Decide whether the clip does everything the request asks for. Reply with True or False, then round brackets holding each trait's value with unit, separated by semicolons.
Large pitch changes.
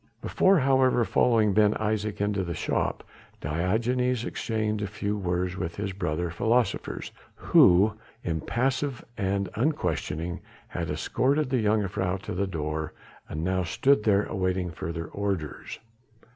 False (4.4 semitones)